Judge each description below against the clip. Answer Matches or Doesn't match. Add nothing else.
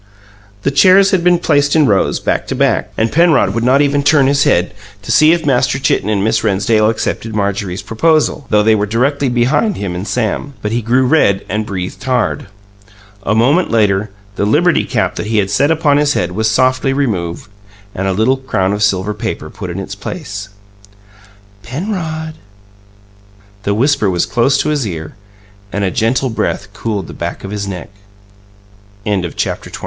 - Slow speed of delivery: Doesn't match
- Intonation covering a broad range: Matches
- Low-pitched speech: Matches